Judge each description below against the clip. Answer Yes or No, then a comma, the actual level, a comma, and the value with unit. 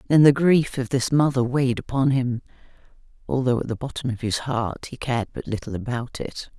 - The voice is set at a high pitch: No, low, 125 Hz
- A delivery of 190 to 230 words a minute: Yes, average, 200 wpm